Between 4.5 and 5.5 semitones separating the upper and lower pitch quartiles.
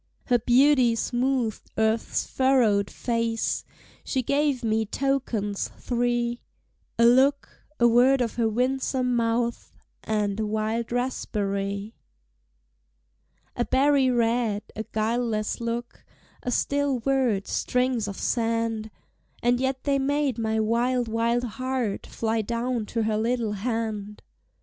No: narrow, 2.5 semitones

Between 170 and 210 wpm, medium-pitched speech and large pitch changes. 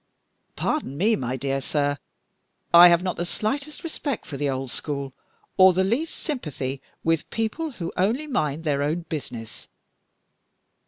No: average, 150 wpm; medium, 165 Hz; wide, 7.9 semitones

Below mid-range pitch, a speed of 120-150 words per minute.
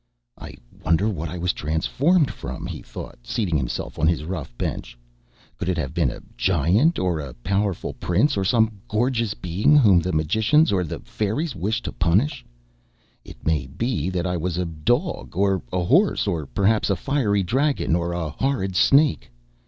No: very low, 95 Hz; average, 175 wpm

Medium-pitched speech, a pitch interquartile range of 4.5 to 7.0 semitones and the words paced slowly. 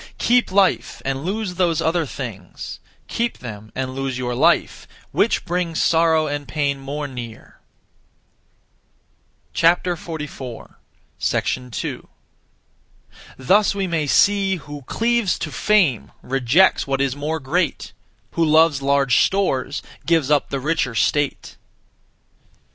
Yes: medium, 150 Hz; average, 4.8 semitones; slow, 115 wpm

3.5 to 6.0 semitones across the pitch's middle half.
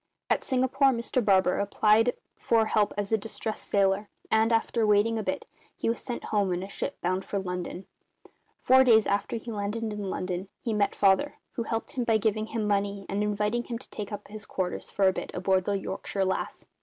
No: narrow, 2.5 semitones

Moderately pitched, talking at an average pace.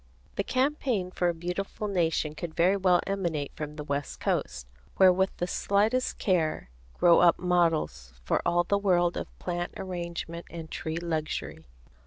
Yes: medium, 175 Hz; average, 160 wpm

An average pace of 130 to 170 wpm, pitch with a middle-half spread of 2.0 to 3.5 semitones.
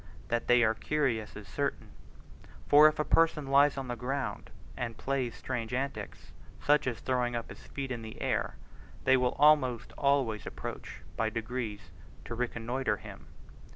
Yes: average, 160 wpm; average, 3.2 semitones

